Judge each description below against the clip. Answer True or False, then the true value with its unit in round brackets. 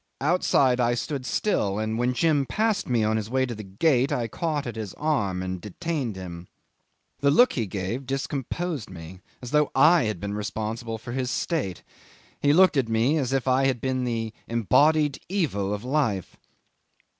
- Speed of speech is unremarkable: True (180 wpm)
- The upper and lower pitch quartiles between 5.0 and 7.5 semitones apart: True (5.3 semitones)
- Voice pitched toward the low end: True (125 Hz)